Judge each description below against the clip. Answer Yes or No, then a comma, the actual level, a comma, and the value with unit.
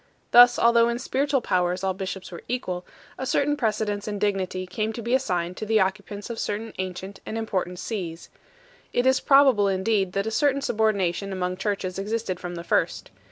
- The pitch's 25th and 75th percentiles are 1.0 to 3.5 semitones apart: No, average, 3.9 semitones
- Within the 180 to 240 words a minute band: Yes, average, 185 wpm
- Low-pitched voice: No, high, 205 Hz